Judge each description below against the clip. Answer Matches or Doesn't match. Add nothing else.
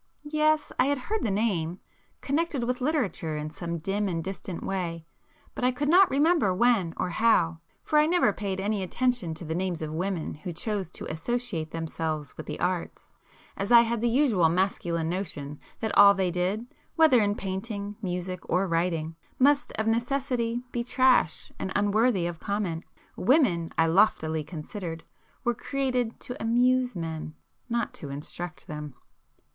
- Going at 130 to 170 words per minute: Matches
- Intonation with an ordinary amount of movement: Doesn't match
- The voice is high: Matches